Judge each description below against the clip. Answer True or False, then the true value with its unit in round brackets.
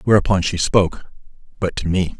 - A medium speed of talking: True (165 wpm)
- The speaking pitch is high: False (90 Hz)